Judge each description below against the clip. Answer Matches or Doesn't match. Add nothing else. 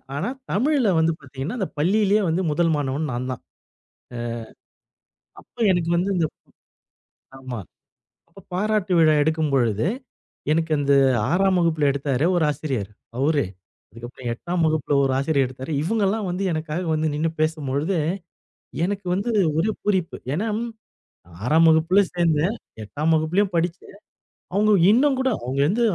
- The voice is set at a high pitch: Doesn't match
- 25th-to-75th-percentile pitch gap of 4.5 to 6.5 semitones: Matches